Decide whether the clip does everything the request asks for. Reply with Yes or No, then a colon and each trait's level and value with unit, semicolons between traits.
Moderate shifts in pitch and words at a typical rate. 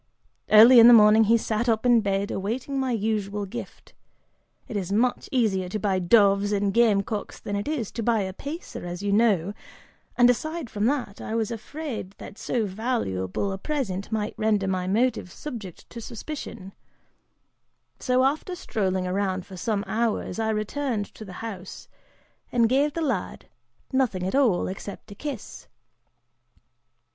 Yes: average, 3.6 semitones; average, 165 wpm